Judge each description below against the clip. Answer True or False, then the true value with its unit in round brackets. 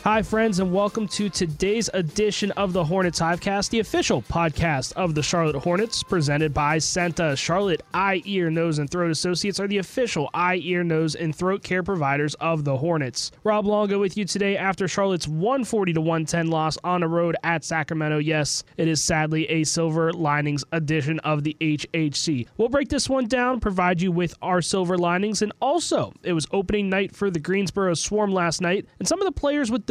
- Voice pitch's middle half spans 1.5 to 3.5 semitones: False (3.9 semitones)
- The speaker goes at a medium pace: True (195 wpm)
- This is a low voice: False (180 Hz)